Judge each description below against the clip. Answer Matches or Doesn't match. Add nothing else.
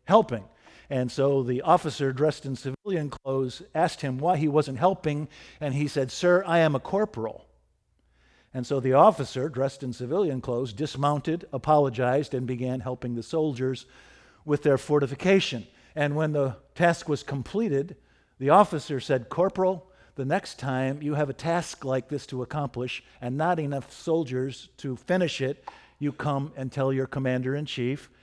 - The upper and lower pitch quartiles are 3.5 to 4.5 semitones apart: Doesn't match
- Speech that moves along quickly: Doesn't match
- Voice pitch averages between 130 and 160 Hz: Matches